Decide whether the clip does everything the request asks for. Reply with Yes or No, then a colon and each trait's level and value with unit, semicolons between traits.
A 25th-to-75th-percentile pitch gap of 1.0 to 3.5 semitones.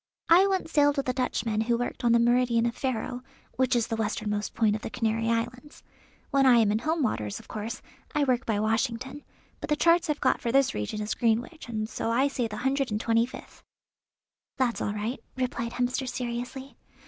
Yes: average, 2.9 semitones